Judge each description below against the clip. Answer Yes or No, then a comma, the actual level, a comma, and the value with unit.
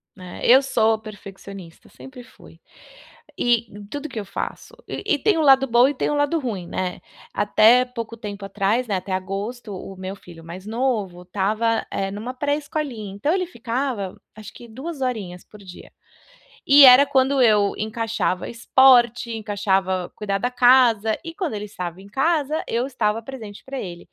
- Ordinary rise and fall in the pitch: Yes, average, 4.7 semitones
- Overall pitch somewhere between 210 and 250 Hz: Yes, high, 225 Hz